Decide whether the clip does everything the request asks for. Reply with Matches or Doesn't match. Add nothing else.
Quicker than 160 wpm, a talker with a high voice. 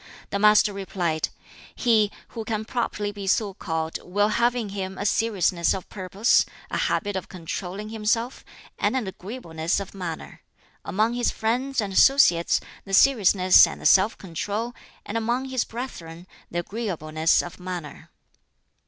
Doesn't match